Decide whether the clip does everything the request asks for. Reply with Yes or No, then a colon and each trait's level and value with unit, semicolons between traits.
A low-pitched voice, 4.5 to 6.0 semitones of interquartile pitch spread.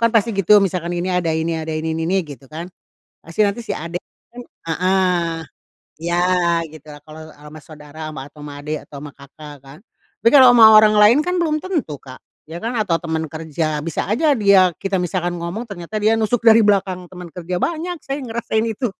No: medium, 180 Hz; average, 5.2 semitones